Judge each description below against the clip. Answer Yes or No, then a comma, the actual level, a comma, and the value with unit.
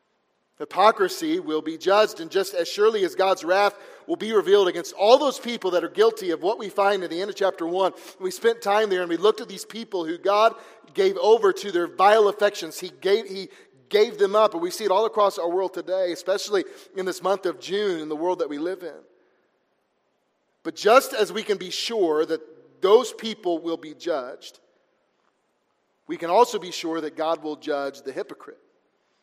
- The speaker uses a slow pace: No, fast, 205 wpm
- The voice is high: Yes, high, 200 Hz